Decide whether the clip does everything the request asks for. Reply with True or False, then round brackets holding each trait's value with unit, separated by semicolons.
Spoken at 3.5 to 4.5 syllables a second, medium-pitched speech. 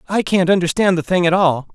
False (5.8 syllables/s; 175 Hz)